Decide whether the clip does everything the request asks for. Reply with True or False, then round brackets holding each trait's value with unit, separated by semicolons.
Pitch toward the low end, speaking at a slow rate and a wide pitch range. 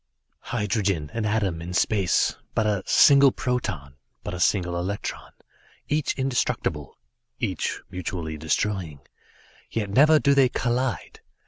True (105 Hz; 120 wpm; 6.1 semitones)